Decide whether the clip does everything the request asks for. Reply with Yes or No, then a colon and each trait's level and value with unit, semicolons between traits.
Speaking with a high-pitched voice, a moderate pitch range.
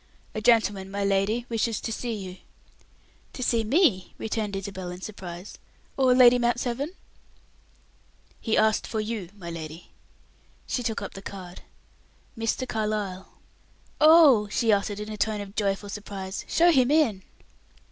Yes: high, 215 Hz; average, 3.5 semitones